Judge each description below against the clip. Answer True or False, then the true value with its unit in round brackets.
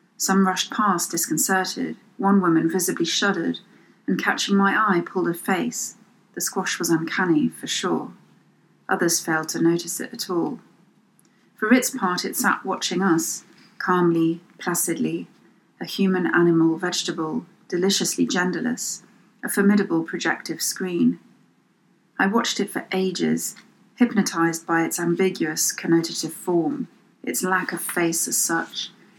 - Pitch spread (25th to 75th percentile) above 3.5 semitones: False (3.1 semitones)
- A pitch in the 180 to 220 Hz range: True (185 Hz)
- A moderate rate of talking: False (130 wpm)